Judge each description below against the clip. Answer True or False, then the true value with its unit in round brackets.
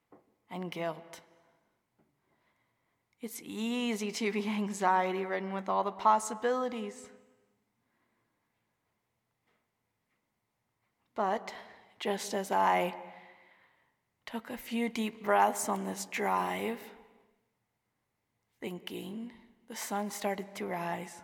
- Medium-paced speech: False (85 wpm)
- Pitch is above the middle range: True (205 Hz)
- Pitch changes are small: False (3.7 semitones)